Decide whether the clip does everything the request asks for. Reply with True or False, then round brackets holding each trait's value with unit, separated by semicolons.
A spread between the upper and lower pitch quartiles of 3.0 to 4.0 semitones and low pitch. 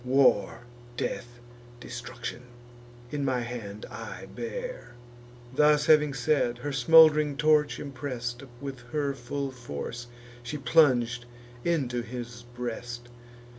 True (3.4 semitones; 125 Hz)